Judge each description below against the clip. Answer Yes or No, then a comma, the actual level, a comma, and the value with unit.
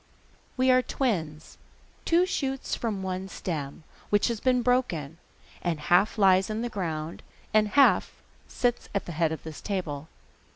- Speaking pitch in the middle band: No, high, 195 Hz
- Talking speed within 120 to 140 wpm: No, average, 155 wpm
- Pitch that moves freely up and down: Yes, wide, 6.9 semitones